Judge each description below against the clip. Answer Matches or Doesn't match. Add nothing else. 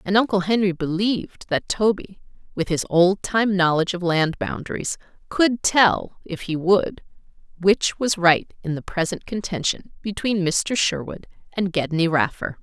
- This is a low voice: Doesn't match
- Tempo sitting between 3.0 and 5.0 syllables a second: Matches